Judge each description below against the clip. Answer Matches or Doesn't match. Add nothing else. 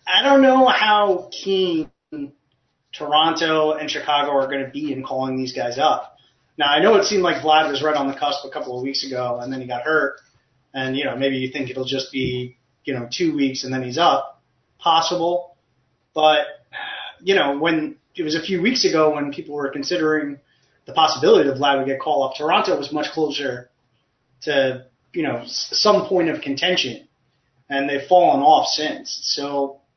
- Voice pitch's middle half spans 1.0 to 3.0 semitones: Doesn't match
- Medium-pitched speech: Matches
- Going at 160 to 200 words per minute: Matches